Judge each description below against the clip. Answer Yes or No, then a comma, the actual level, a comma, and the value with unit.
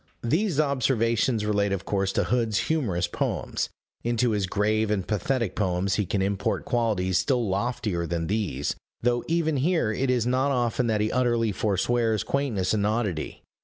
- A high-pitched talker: No, low, 110 Hz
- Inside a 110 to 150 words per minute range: No, average, 165 wpm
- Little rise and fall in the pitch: No, average, 4.0 semitones